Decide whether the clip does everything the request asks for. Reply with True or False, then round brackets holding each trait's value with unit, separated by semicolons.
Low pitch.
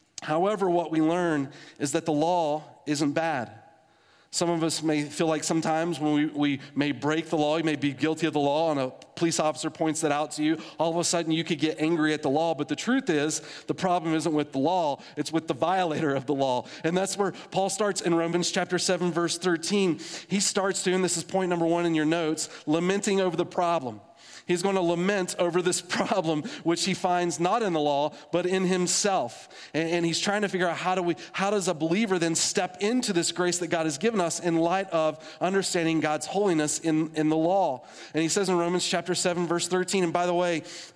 False (170 Hz)